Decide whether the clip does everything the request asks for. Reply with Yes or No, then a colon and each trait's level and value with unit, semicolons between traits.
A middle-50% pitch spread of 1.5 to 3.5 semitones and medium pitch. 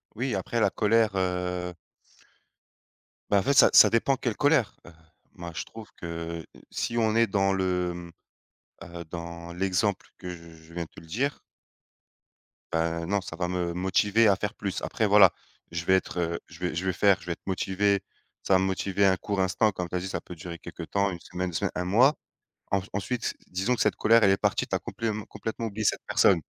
No: average, 3.1 semitones; very low, 95 Hz